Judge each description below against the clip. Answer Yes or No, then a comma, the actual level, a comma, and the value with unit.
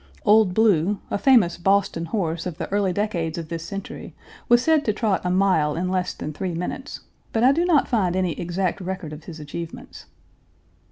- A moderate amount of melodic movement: Yes, average, 3.8 semitones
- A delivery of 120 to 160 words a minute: No, average, 190 wpm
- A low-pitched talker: No, medium, 185 Hz